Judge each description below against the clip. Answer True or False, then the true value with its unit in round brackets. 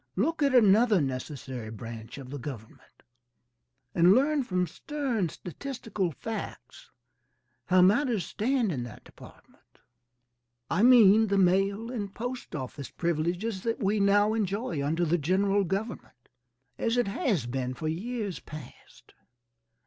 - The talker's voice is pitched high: True (195 Hz)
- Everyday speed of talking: False (125 wpm)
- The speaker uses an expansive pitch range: True (6.7 semitones)